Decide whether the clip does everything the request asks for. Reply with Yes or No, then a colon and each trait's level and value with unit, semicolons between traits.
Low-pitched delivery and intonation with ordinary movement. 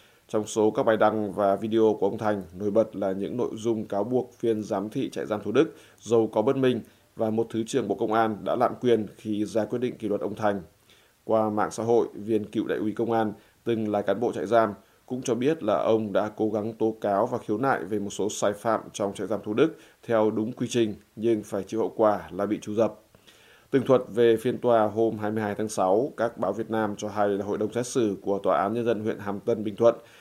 No: low, 110 Hz; narrow, 1.6 semitones